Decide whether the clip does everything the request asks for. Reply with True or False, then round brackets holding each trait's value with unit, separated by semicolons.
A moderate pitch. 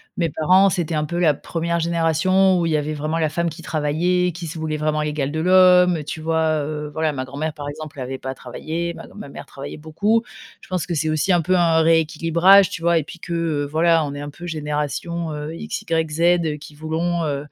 True (160 Hz)